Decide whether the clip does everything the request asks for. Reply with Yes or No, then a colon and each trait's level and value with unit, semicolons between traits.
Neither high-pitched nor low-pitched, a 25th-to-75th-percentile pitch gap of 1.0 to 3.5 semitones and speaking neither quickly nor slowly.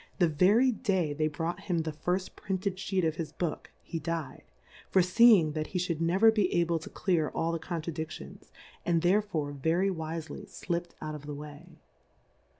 Yes: medium, 170 Hz; average, 2.9 semitones; average, 170 wpm